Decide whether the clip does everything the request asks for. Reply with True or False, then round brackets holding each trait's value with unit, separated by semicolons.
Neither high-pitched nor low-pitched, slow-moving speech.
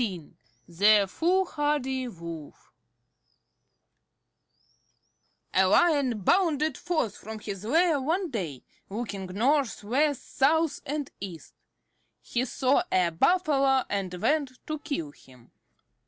False (255 Hz; 105 wpm)